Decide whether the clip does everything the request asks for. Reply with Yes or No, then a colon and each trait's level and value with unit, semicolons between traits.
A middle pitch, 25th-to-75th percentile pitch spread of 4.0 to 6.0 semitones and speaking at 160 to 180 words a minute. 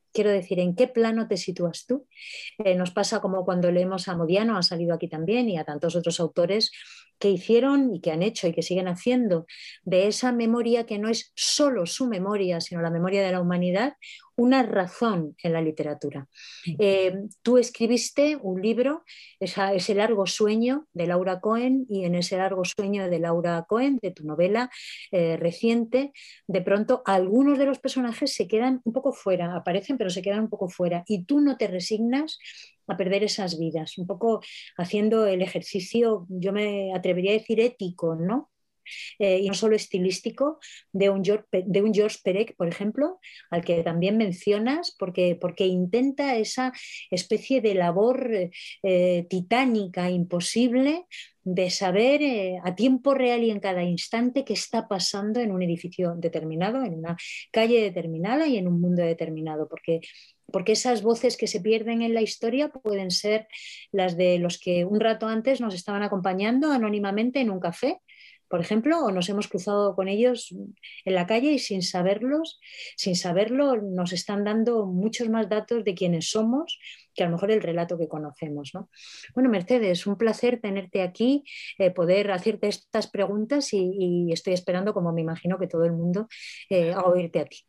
No: high, 200 Hz; average, 4.4 semitones; average, 175 wpm